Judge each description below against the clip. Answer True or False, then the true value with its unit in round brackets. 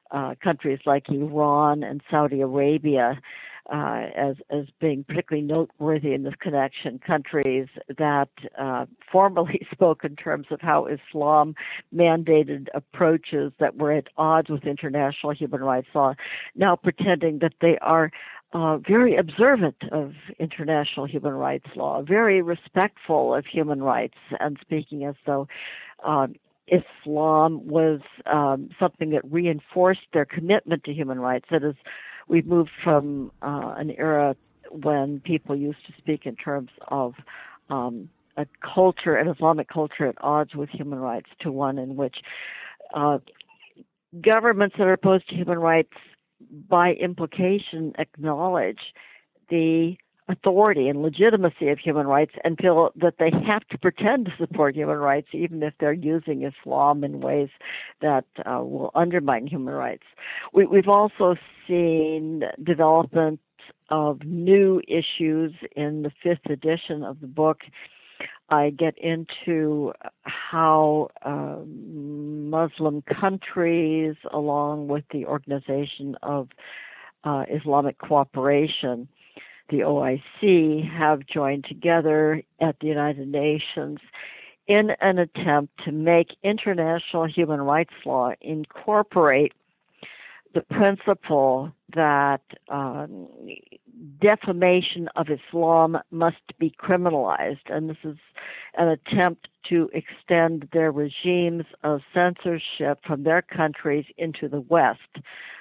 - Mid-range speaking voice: True (155 Hz)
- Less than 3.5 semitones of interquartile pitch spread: True (2.7 semitones)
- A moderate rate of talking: False (125 wpm)